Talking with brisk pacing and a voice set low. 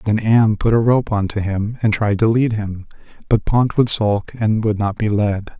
Yes: fast, 235 wpm; low, 110 Hz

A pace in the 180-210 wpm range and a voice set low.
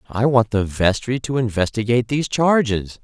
No: average, 160 wpm; low, 115 Hz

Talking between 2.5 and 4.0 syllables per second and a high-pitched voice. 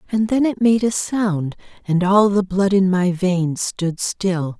Yes: 3.7 syllables/s; high, 195 Hz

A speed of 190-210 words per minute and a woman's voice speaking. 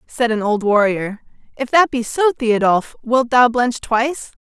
No: average, 175 wpm; female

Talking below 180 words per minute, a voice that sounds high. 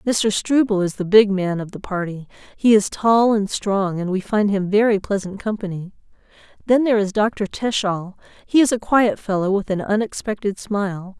No: average, 190 wpm; high, 205 Hz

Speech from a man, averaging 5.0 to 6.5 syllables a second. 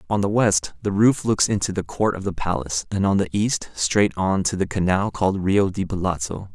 Yes: male; 5.2 syllables/s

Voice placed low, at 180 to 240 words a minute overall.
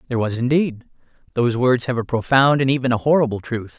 Yes: low, 125 Hz; fast, 205 wpm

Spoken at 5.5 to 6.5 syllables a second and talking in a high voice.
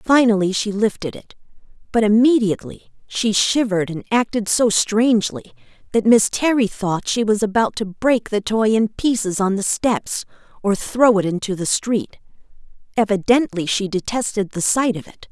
No: 4.8 syllables/s; high, 210 Hz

